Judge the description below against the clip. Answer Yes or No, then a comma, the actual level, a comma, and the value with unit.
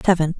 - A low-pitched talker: No, medium, 170 Hz